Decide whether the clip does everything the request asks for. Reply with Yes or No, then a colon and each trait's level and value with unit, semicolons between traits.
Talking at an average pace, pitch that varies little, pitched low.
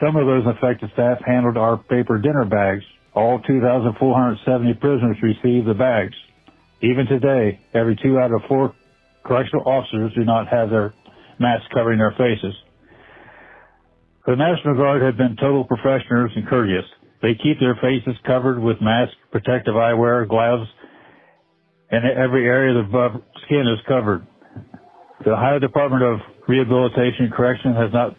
Yes: average, 150 wpm; narrow, 2.3 semitones; low, 125 Hz